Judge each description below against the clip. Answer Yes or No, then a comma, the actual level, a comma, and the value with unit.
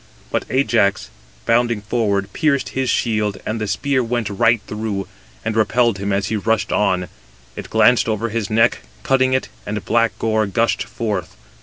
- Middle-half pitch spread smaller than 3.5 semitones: Yes, narrow, 2.6 semitones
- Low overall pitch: Yes, low, 110 Hz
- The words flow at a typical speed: Yes, average, 165 wpm